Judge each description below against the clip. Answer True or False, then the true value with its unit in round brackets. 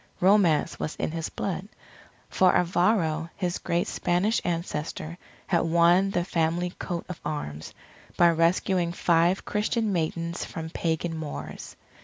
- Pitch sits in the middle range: True (170 Hz)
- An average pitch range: False (1.8 semitones)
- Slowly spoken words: True (130 wpm)